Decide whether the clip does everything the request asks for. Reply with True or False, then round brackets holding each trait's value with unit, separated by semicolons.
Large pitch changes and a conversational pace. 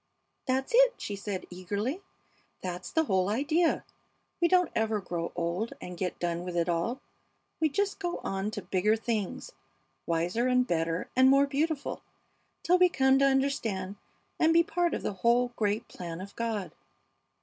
True (7.2 semitones; 170 wpm)